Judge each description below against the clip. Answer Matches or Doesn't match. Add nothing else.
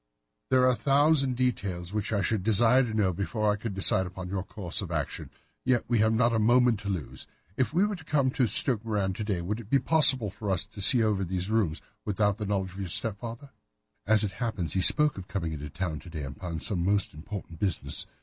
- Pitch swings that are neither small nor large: Matches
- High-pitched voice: Doesn't match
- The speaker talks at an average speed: Doesn't match